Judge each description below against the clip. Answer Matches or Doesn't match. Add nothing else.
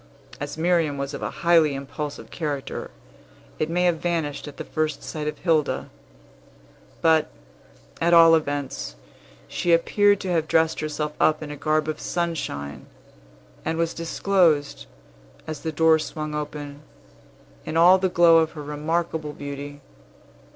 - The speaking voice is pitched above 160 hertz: Doesn't match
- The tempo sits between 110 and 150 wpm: Matches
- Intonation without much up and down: Matches